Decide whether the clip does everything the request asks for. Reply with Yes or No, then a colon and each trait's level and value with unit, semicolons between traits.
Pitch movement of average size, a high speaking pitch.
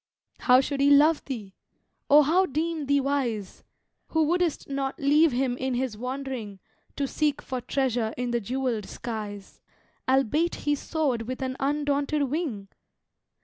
Yes: average, 3.1 semitones; very high, 270 Hz